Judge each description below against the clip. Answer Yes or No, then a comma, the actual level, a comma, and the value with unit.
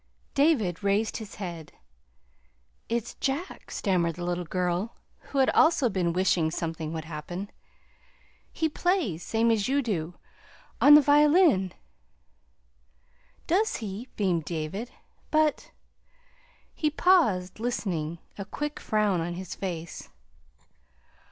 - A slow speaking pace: Yes, slow, 120 wpm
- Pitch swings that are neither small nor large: No, wide, 8.4 semitones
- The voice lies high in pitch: Yes, high, 200 Hz